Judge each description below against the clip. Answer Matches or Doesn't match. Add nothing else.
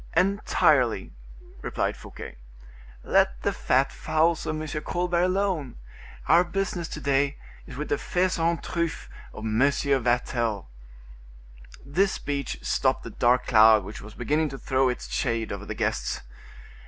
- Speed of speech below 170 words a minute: Matches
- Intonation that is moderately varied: Doesn't match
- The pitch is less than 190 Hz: Matches